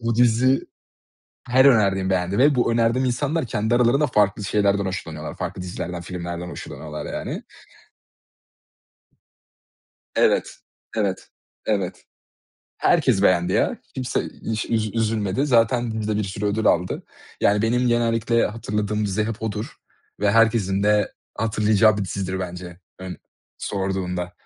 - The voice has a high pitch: No, low, 105 Hz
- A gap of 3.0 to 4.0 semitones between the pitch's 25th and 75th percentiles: Yes, average, 3.3 semitones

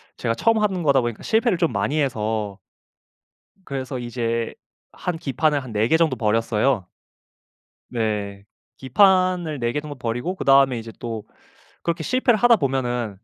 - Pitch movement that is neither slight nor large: No, wide, 6.0 semitones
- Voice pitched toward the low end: Yes, low, 130 Hz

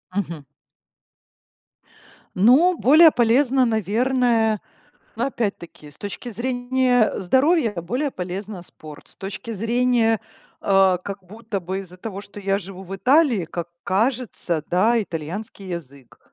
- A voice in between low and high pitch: No, high, 210 Hz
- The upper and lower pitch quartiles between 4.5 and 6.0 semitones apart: Yes, average, 5.0 semitones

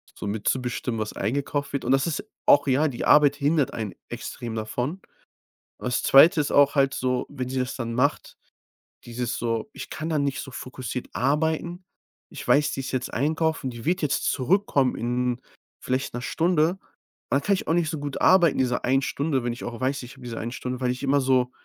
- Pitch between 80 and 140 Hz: Yes, low, 135 Hz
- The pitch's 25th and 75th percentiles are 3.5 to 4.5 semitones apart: No, average, 3.0 semitones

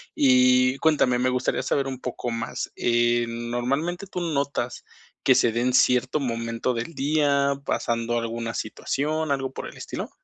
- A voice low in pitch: Yes, low, 125 Hz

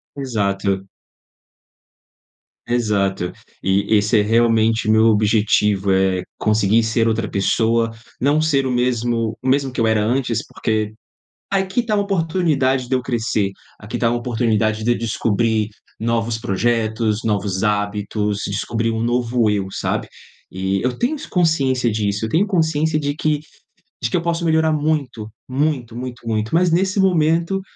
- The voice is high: No, low, 115 Hz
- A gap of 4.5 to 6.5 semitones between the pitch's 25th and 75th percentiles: Yes, average, 4.8 semitones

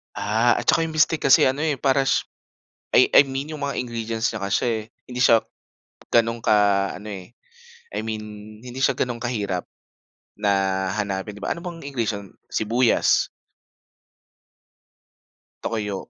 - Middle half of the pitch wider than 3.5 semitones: Yes, average, 4.0 semitones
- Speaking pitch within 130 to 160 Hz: No, low, 115 Hz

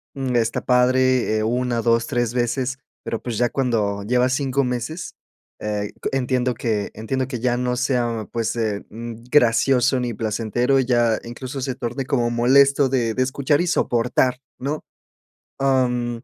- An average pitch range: No, narrow, 2.0 semitones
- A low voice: Yes, low, 125 Hz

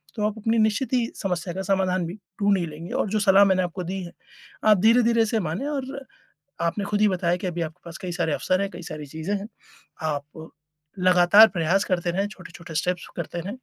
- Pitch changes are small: No, average, 3.2 semitones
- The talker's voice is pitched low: No, medium, 185 Hz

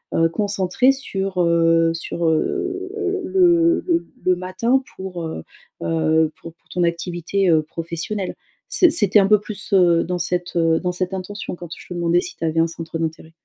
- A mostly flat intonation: No, average, 3.5 semitones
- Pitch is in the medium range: Yes, medium, 180 Hz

